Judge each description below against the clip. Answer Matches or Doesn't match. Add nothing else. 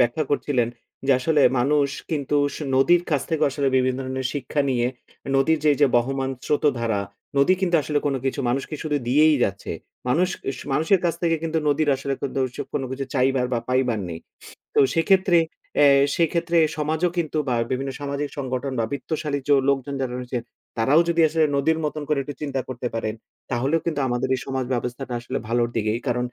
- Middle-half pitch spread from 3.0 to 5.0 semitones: Matches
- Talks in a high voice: Doesn't match